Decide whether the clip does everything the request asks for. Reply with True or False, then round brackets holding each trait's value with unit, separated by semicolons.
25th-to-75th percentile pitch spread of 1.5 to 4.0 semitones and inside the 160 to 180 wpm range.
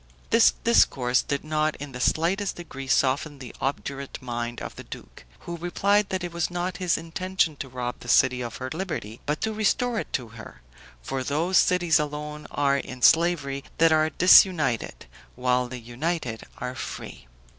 False (5.4 semitones; 175 wpm)